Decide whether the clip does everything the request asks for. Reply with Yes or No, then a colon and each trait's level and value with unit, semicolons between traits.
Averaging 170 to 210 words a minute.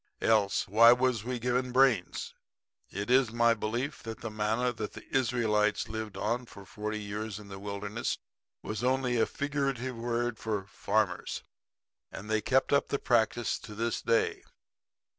No: average, 160 wpm